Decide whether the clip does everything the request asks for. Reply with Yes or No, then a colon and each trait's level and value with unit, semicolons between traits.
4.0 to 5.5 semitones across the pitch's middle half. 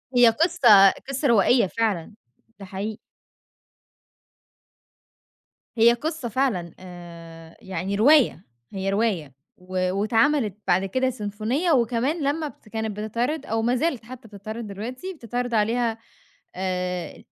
Yes: average, 4.5 semitones